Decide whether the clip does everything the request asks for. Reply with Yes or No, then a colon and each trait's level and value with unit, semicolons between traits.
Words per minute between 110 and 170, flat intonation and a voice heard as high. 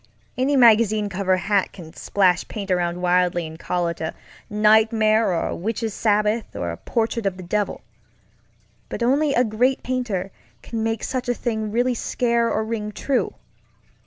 No: average, 160 wpm; average, 4.0 semitones; high, 215 Hz